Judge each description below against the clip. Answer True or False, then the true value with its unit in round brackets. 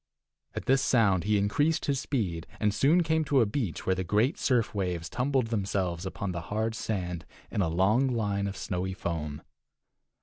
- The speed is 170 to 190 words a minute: True (180 wpm)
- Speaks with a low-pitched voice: True (100 Hz)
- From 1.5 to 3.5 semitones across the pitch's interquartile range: False (5.2 semitones)